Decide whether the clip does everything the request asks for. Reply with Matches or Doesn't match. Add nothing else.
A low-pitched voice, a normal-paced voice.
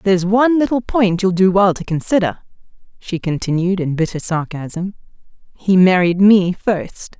Doesn't match